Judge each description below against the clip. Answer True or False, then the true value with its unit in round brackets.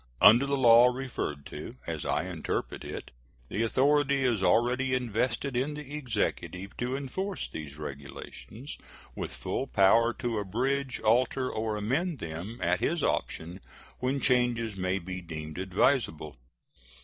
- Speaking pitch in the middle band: False (120 Hz)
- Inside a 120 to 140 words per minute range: True (135 wpm)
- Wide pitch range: True (5.7 semitones)